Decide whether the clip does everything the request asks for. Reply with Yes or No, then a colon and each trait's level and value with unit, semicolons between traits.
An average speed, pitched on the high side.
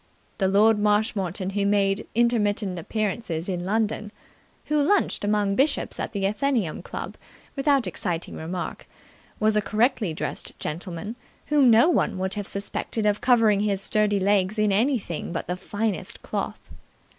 Yes: average, 145 wpm; high, 205 Hz